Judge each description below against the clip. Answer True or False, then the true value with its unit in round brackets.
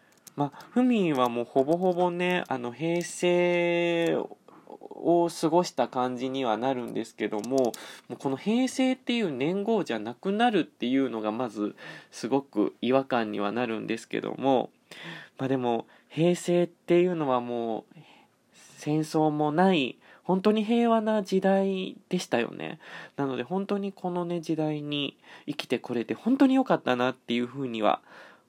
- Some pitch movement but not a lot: False (6.5 semitones)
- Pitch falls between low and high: True (155 Hz)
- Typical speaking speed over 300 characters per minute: False (295 characters per minute)